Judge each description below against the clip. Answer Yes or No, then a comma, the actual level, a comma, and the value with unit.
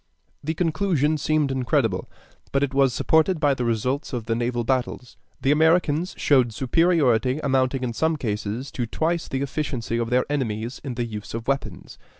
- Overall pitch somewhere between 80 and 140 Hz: Yes, low, 135 Hz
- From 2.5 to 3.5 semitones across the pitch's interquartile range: No, average, 4.1 semitones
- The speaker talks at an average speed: Yes, average, 170 wpm